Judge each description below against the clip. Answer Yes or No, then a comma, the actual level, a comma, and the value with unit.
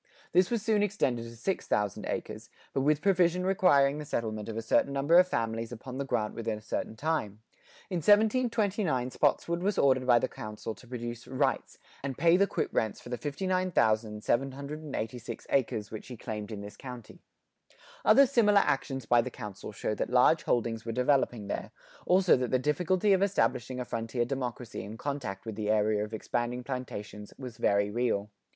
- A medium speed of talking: Yes, average, 180 wpm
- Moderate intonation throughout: No, wide, 6.2 semitones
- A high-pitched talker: No, low, 125 Hz